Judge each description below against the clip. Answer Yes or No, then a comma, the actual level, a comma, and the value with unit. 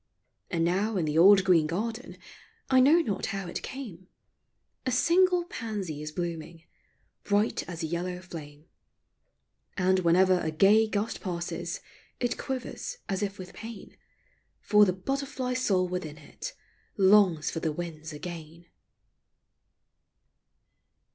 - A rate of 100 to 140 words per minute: Yes, slow, 135 wpm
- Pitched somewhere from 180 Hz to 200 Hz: Yes, medium, 185 Hz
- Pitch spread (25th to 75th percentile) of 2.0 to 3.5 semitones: No, average, 4.7 semitones